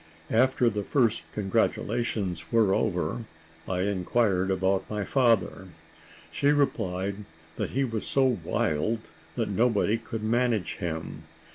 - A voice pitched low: Yes, low, 110 Hz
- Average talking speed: No, slow, 120 wpm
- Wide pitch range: No, average, 3.8 semitones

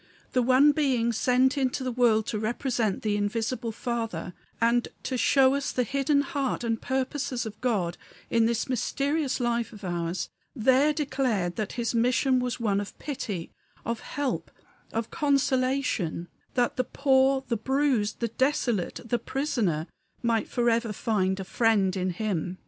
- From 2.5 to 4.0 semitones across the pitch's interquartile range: Yes, average, 3.6 semitones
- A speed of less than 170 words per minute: Yes, average, 155 wpm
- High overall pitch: Yes, high, 240 Hz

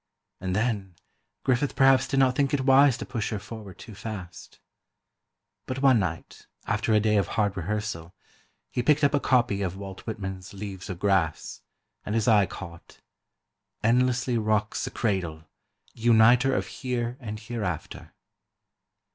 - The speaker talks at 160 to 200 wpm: No, average, 150 wpm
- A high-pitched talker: No, low, 110 Hz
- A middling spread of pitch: Yes, average, 4.4 semitones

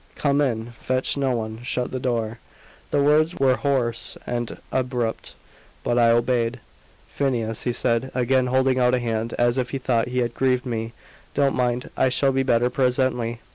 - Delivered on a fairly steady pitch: Yes, narrow, 1.9 semitones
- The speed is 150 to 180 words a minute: Yes, average, 175 wpm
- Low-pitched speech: Yes, low, 125 Hz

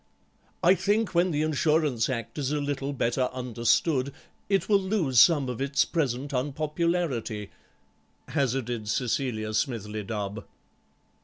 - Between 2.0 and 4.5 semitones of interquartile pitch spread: No, average, 5.1 semitones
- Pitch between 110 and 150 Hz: Yes, low, 135 Hz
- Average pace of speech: No, slow, 125 wpm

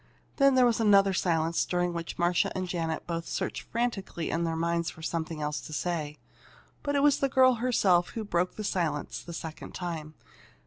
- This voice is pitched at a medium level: Yes, medium, 175 Hz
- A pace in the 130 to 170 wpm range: No, average, 190 wpm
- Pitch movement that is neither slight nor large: Yes, average, 4.7 semitones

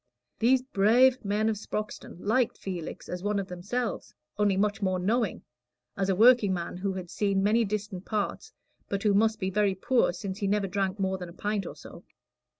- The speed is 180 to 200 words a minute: Yes, average, 190 wpm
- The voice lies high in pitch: Yes, high, 200 Hz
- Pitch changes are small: Yes, narrow, 2.3 semitones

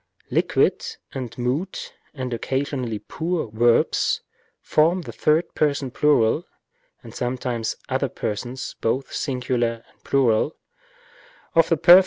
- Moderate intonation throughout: Yes, average, 4.2 semitones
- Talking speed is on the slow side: Yes, slow, 115 wpm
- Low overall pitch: Yes, low, 130 Hz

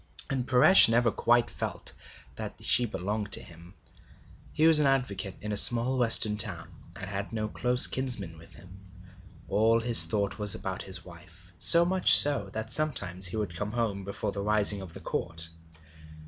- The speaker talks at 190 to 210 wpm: No, average, 175 wpm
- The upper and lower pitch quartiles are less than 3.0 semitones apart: No, average, 4.1 semitones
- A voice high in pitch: No, low, 105 Hz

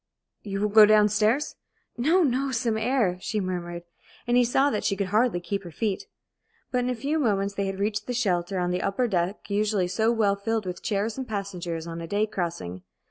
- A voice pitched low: No, high, 205 Hz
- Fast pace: Yes, fast, 215 wpm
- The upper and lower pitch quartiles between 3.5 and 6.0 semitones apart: Yes, average, 3.8 semitones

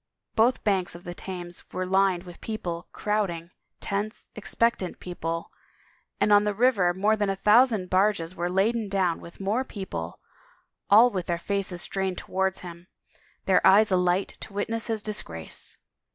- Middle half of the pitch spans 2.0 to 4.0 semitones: Yes, average, 3.0 semitones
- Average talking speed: Yes, average, 155 wpm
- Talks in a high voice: Yes, high, 195 Hz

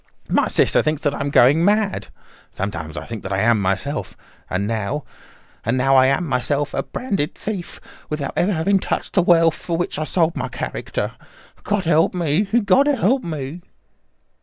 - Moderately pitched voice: Yes, medium, 155 Hz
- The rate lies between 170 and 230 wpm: Yes, average, 175 wpm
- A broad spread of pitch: Yes, wide, 5.9 semitones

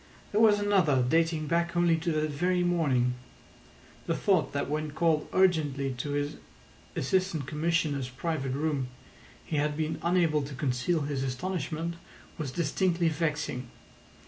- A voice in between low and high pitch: Yes, medium, 155 Hz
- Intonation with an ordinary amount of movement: Yes, average, 3.2 semitones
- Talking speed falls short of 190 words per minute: Yes, average, 140 wpm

